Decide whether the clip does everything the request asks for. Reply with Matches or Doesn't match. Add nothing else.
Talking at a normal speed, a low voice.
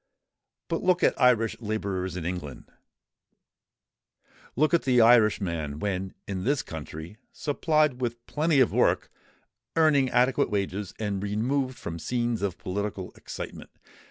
Doesn't match